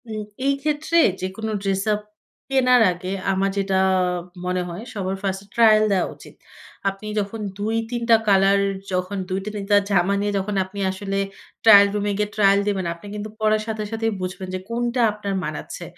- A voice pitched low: No, high, 205 Hz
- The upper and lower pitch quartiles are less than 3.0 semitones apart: Yes, narrow, 2.4 semitones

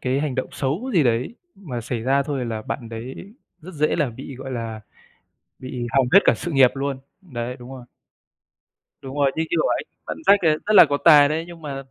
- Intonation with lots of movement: No, average, 3.9 semitones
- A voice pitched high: No, low, 135 Hz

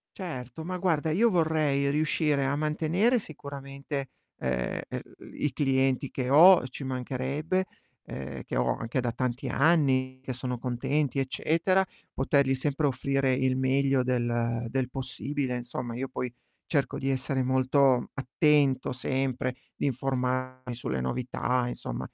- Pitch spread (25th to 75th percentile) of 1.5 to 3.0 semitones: Yes, narrow, 2.4 semitones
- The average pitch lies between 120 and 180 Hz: Yes, low, 135 Hz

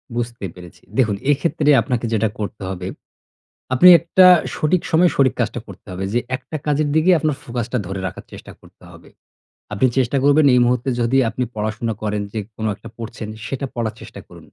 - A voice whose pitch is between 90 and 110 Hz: No, low, 120 Hz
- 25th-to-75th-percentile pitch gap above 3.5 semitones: Yes, average, 4.7 semitones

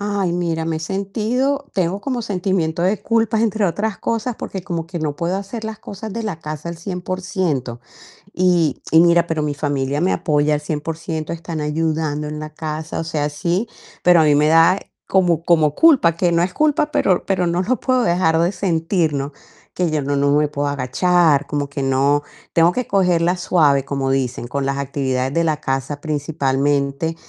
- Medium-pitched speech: Yes, medium, 165 Hz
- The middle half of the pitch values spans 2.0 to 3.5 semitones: No, average, 4.1 semitones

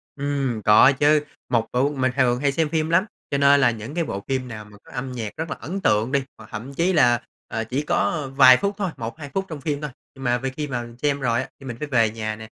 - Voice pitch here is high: No, low, 135 Hz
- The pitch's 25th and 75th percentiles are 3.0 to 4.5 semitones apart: Yes, average, 3.8 semitones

